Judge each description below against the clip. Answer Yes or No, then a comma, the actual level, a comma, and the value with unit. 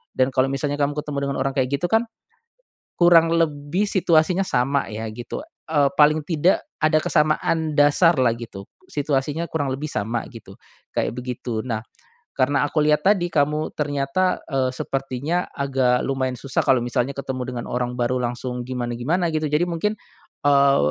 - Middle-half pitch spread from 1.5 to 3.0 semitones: No, average, 3.5 semitones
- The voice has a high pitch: No, medium, 140 Hz